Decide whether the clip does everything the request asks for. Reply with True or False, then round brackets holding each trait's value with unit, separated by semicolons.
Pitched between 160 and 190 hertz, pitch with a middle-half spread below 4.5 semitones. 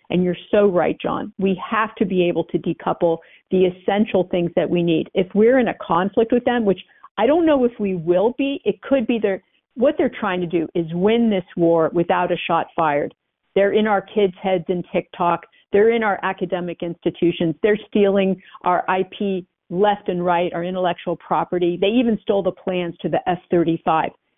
True (185 Hz; 3.2 semitones)